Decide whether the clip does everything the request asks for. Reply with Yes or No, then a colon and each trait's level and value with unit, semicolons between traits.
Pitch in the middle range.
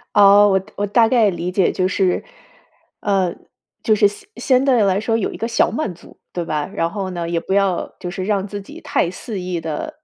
No: high, 195 Hz